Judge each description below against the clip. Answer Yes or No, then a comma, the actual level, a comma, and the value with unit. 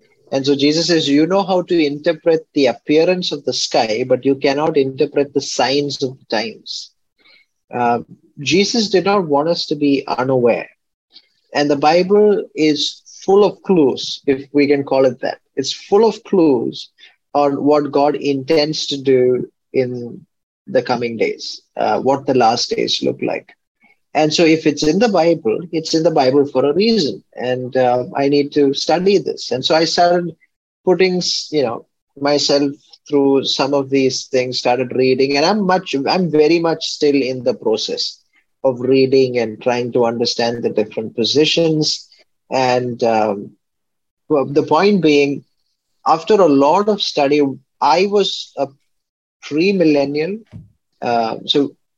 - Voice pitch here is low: No, medium, 145 Hz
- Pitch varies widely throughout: No, average, 4.1 semitones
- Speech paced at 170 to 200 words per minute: No, average, 160 wpm